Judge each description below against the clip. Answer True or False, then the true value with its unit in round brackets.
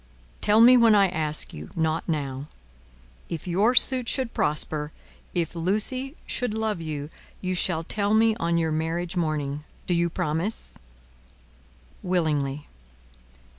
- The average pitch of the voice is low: False (170 Hz)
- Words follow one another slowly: True (130 wpm)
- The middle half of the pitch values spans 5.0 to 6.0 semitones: True (5.4 semitones)